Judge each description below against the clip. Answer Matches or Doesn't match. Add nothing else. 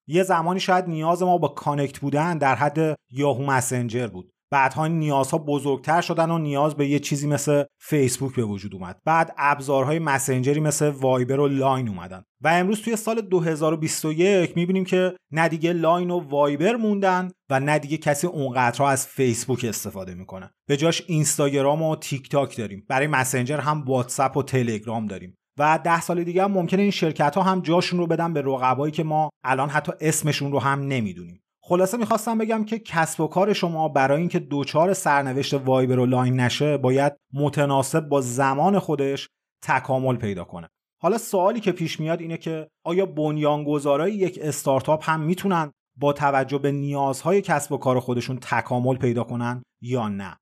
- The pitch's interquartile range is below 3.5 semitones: Doesn't match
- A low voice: Doesn't match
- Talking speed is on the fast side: Matches